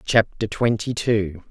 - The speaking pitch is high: No, low, 105 Hz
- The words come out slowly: Yes, slow, 120 wpm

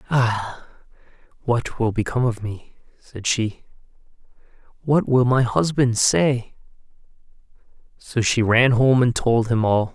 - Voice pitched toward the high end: No, low, 120 Hz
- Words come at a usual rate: No, slow, 125 wpm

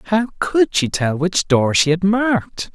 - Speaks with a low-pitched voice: No, medium, 185 Hz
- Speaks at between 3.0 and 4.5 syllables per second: Yes, 4.1 syllables/s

